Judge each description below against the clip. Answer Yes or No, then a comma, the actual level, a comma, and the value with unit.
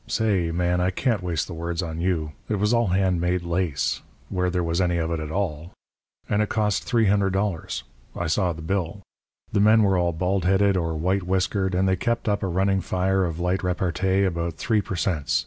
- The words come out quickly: Yes, fast, 210 wpm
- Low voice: Yes, very low, 90 Hz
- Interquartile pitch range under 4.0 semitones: Yes, narrow, 2.5 semitones